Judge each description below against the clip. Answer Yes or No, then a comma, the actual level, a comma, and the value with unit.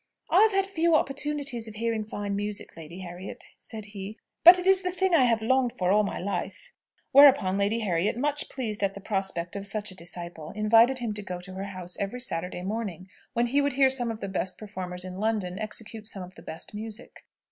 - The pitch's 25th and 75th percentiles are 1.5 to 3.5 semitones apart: No, average, 4.8 semitones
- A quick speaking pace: Yes, fast, 220 wpm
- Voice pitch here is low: No, high, 210 Hz